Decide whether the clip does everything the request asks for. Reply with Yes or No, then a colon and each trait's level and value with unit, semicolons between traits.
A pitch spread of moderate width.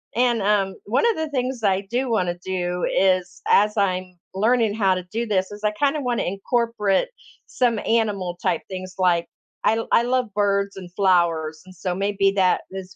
Yes: average, 3.7 semitones